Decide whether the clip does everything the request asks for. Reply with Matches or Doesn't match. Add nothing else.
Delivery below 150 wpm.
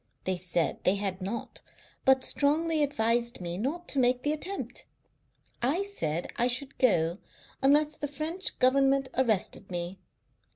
Matches